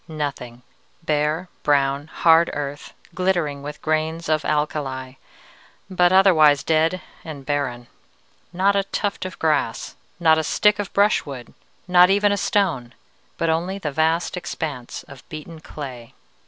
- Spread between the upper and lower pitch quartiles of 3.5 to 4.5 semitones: Yes, average, 3.8 semitones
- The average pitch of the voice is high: No, medium, 155 Hz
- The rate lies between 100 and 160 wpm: Yes, slow, 135 wpm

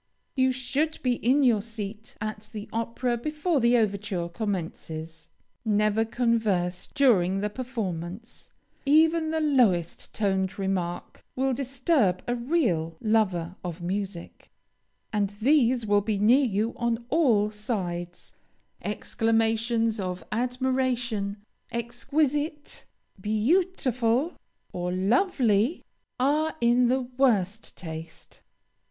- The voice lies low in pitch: No, high, 225 Hz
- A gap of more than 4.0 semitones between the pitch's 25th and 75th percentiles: Yes, average, 4.6 semitones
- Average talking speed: No, slow, 105 wpm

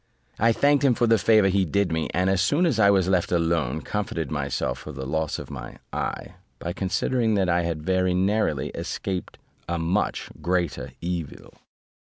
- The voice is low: Yes, very low, 90 Hz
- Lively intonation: No, average, 3.5 semitones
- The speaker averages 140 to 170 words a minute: No, average, 185 wpm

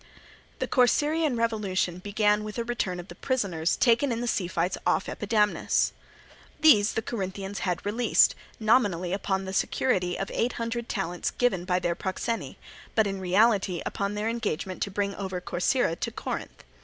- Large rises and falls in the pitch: No, average, 3.9 semitones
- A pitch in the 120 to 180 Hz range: No, high, 205 Hz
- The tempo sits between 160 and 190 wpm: Yes, average, 165 wpm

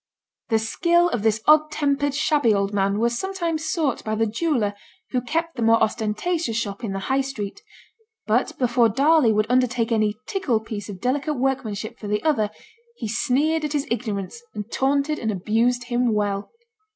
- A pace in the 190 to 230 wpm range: No, average, 175 wpm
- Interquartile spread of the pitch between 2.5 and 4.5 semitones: No, average, 5.2 semitones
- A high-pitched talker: Yes, high, 240 Hz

